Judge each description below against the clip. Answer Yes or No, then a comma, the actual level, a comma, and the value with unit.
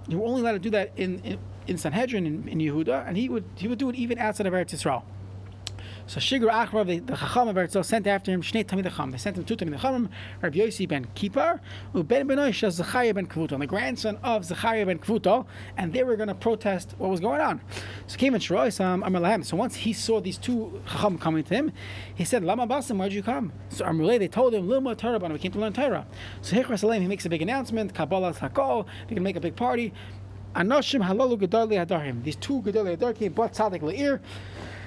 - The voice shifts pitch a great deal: Yes, wide, 6.1 semitones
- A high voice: Yes, high, 200 Hz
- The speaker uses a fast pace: Yes, fast, 220 wpm